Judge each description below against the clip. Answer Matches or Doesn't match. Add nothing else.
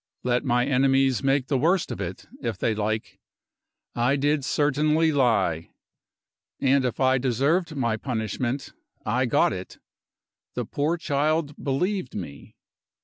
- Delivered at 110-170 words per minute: Matches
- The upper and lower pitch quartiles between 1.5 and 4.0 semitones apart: Matches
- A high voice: Doesn't match